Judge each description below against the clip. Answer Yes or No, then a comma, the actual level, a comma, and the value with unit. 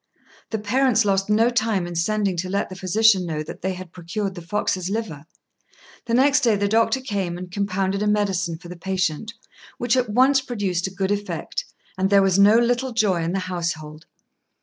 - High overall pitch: Yes, high, 200 Hz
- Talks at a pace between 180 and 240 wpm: Yes, average, 195 wpm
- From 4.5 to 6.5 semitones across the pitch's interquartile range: No, average, 3.5 semitones